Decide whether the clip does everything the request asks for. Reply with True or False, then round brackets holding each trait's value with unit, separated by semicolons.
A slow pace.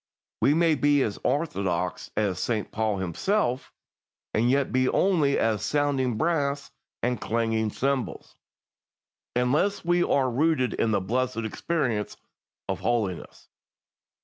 True (120 wpm)